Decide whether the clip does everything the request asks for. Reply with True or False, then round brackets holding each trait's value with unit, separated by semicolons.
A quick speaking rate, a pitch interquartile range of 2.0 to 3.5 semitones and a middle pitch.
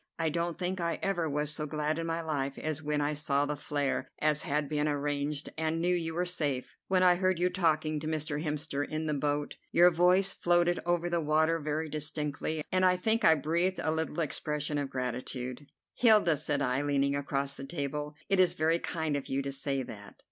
True (210 wpm; 2.7 semitones; 155 Hz)